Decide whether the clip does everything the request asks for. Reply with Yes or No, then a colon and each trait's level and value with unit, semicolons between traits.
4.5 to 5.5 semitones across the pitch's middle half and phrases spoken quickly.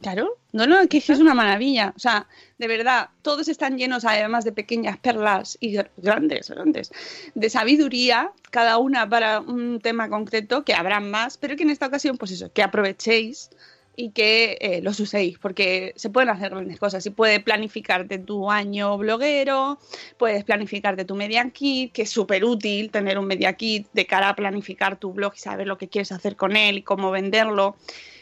No: average, 3.7 semitones; fast, 195 wpm